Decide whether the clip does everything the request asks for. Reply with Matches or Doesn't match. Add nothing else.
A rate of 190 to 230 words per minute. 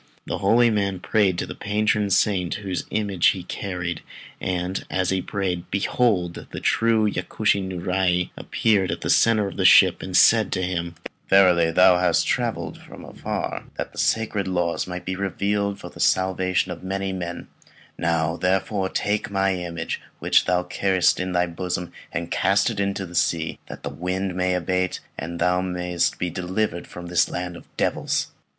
Doesn't match